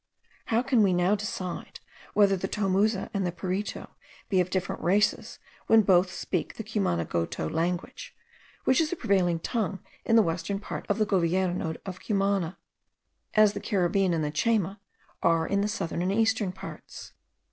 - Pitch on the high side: Yes, high, 195 Hz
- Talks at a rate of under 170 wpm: Yes, average, 160 wpm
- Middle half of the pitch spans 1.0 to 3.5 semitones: Yes, average, 3.1 semitones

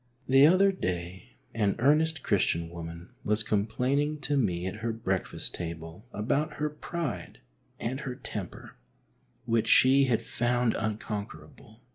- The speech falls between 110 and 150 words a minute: Yes, slow, 135 wpm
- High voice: No, low, 115 Hz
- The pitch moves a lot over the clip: Yes, wide, 6.3 semitones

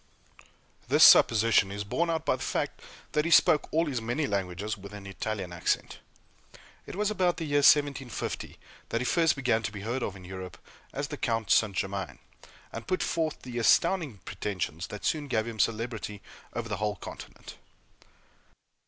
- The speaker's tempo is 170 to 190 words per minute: Yes, average, 175 wpm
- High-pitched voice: No, low, 115 Hz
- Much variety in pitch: Yes, wide, 6.2 semitones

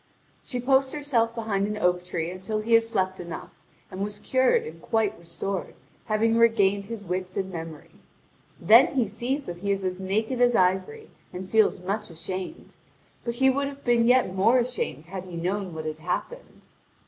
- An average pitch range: Yes, average, 4.4 semitones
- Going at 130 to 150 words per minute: No, average, 185 wpm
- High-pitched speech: Yes, high, 205 Hz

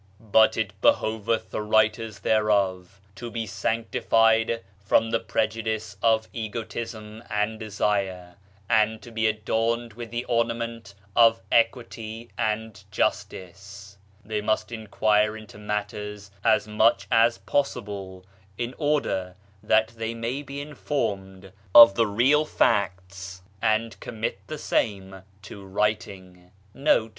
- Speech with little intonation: Yes, narrow, 2.3 semitones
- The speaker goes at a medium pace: No, slow, 120 wpm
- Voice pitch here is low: Yes, low, 110 Hz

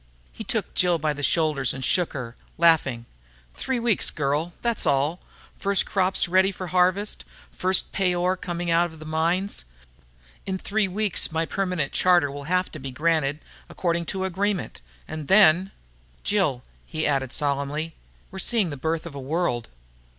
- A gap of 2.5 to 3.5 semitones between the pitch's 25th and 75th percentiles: No, average, 4.3 semitones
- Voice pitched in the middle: Yes, medium, 170 Hz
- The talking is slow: No, average, 165 wpm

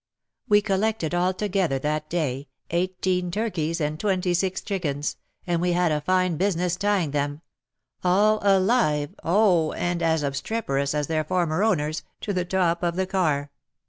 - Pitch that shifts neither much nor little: Yes, average, 3.7 semitones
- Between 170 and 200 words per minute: No, average, 160 wpm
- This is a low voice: No, medium, 175 Hz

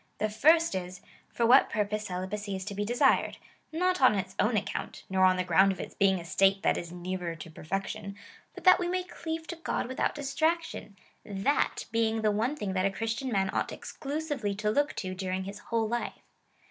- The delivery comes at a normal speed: No, fast, 215 wpm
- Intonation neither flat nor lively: No, wide, 6.0 semitones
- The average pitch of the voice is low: No, high, 210 Hz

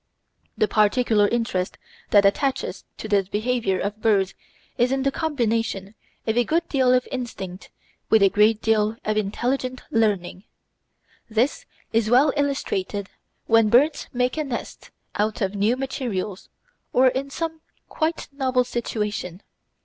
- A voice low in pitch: No, high, 225 Hz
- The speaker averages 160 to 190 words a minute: No, average, 140 wpm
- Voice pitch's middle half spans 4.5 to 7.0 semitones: No, average, 3.8 semitones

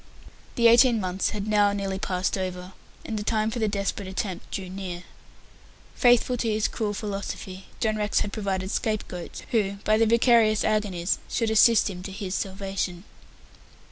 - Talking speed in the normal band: Yes, average, 170 wpm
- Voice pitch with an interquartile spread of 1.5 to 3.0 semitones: Yes, narrow, 2.5 semitones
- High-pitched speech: Yes, high, 205 Hz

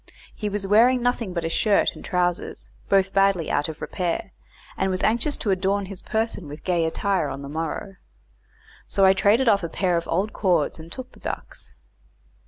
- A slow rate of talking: No, average, 190 wpm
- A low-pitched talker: No, high, 190 Hz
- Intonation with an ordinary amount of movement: Yes, average, 3.5 semitones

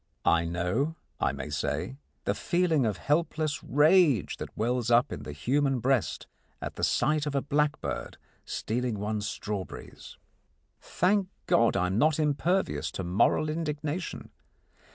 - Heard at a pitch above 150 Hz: No, low, 135 Hz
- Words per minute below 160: Yes, average, 140 wpm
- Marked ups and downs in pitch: Yes, wide, 6.7 semitones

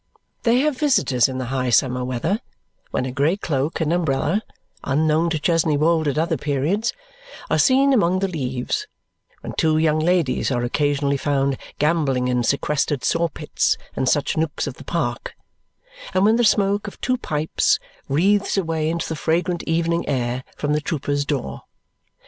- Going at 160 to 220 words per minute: Yes, average, 165 wpm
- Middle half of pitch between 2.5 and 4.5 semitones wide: Yes, average, 4.1 semitones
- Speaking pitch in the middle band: Yes, medium, 155 Hz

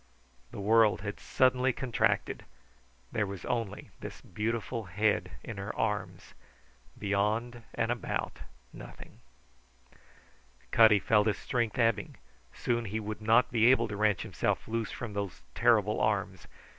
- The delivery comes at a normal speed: No, slow, 130 wpm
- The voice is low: Yes, low, 110 Hz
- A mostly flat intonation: Yes, narrow, 2.1 semitones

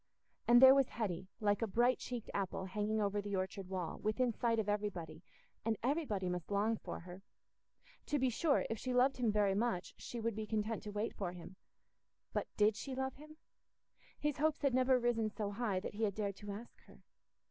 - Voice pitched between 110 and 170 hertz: No, high, 215 Hz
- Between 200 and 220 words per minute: Yes, fast, 205 wpm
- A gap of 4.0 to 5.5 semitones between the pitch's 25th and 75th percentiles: No, average, 3.6 semitones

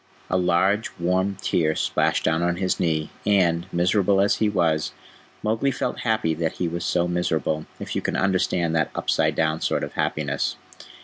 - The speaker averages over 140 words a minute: Yes, average, 175 wpm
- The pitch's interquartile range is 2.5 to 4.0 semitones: Yes, average, 3.1 semitones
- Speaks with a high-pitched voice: No, very low, 90 Hz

